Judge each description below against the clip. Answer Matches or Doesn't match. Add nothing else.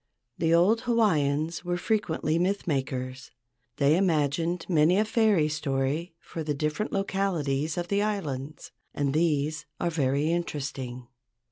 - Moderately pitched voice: Matches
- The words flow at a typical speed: Doesn't match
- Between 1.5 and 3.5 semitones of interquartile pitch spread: Doesn't match